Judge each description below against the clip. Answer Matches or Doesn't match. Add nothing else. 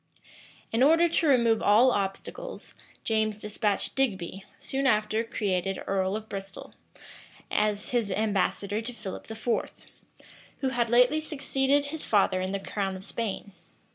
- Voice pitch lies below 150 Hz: Doesn't match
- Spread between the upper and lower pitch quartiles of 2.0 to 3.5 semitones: Doesn't match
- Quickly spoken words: Doesn't match